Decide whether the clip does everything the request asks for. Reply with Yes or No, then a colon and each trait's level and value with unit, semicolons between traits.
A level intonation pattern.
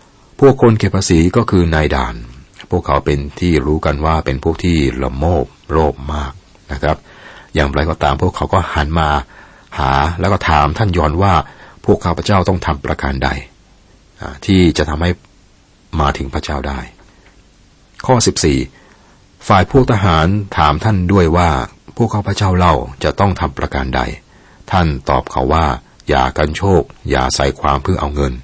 No: average, 4.4 semitones